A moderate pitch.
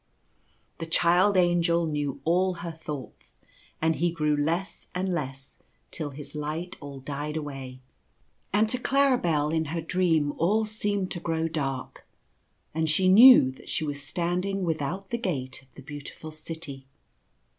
Yes: medium, 160 Hz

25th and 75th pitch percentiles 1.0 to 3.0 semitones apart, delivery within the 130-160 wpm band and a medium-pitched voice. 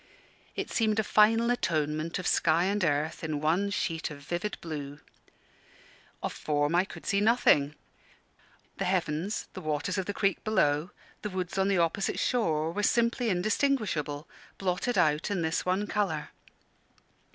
No: average, 5.0 semitones; average, 150 wpm; medium, 180 Hz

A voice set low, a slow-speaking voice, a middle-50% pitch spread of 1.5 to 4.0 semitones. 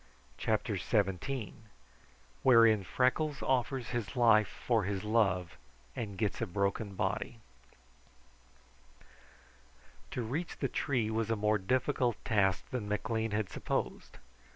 Yes: low, 110 Hz; slow, 115 wpm; average, 3.2 semitones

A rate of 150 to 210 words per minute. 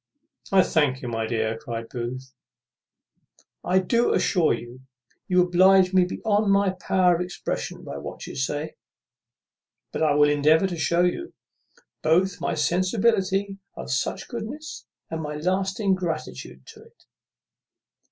No: average, 140 wpm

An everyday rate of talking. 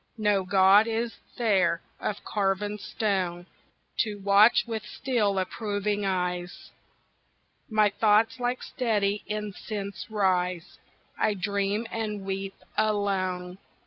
No: slow, 105 wpm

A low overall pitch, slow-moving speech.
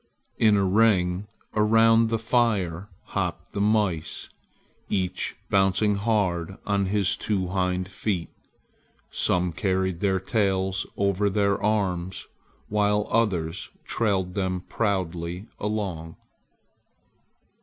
Yes: very low, 95 Hz; slow, 100 wpm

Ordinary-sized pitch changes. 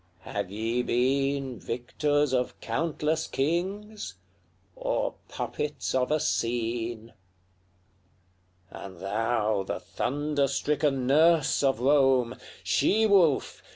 Yes: average, 4.4 semitones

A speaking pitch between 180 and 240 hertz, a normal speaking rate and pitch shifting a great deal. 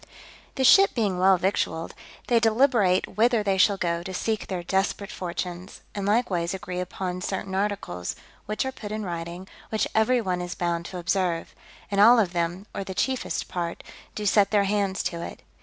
No: high, 190 Hz; average, 185 wpm; average, 3.0 semitones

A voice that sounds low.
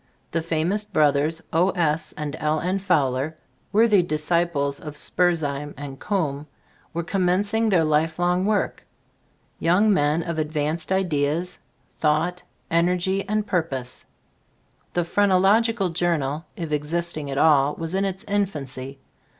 No: medium, 165 Hz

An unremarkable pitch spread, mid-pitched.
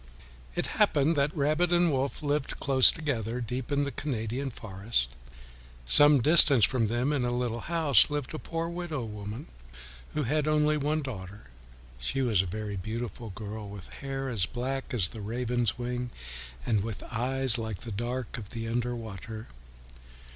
No: average, 4.4 semitones; low, 125 Hz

